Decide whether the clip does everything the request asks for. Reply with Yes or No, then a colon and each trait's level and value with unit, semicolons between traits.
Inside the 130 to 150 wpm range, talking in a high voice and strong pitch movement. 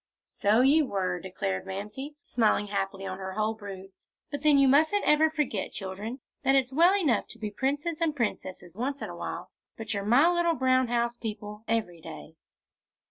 No: average, 185 wpm; high, 230 Hz; wide, 6.2 semitones